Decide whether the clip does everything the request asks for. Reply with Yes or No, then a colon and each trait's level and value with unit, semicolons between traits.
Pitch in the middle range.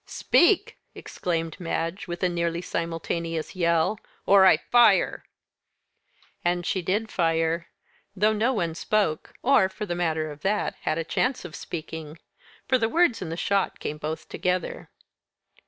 Yes: medium, 175 Hz